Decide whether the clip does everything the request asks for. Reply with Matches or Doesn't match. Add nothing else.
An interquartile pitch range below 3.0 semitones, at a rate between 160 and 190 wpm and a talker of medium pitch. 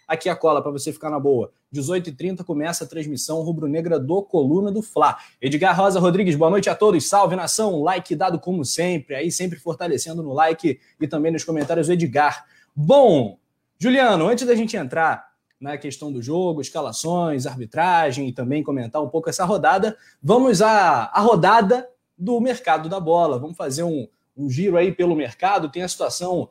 Doesn't match